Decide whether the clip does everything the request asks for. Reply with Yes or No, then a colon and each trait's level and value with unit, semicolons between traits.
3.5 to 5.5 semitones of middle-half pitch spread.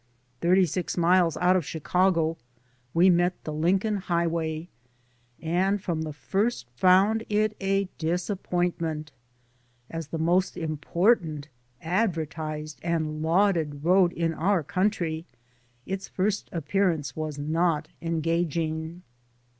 No: average, 2.8 semitones